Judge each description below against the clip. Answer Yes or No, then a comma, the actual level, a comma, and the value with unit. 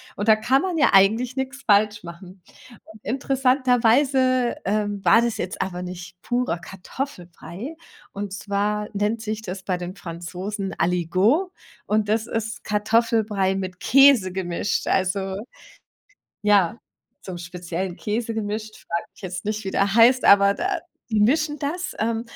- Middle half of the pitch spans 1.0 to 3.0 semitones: No, average, 3.9 semitones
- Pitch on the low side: No, high, 210 Hz